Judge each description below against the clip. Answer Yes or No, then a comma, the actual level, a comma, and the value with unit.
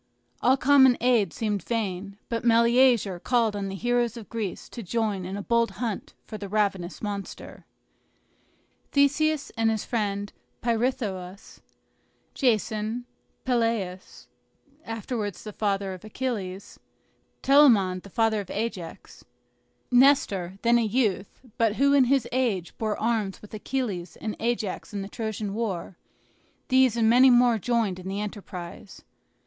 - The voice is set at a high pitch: Yes, high, 220 Hz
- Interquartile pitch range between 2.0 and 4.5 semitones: Yes, average, 3.3 semitones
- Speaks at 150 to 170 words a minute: No, slow, 135 wpm